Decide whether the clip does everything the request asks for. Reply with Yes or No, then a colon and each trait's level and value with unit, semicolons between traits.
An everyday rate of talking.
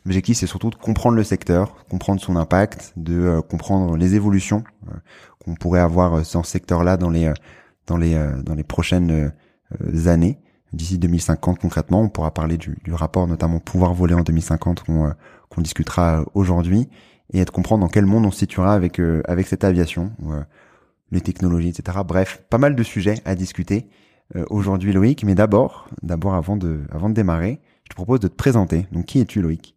Yes: average, 200 wpm